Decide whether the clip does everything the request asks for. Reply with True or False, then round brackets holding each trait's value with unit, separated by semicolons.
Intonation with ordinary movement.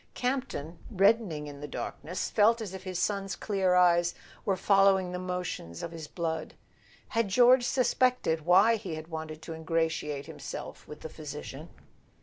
True (4.0 semitones)